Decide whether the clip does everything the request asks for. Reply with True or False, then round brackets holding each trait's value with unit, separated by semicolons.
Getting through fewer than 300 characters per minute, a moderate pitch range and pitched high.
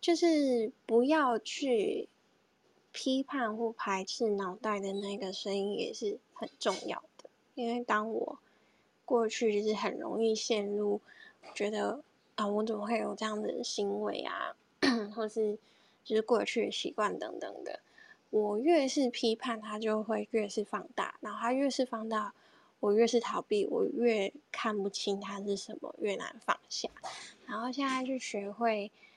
True (220 characters per minute; 3.0 semitones; 220 Hz)